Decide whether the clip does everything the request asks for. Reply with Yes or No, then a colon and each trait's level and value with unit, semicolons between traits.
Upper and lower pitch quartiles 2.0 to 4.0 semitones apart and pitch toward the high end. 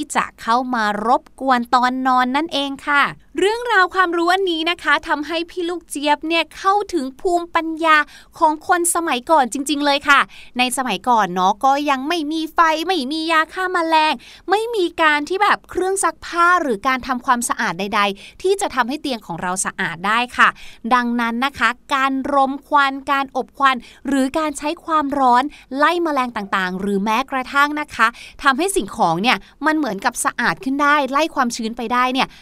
No: average, 4.4 semitones; very high, 280 Hz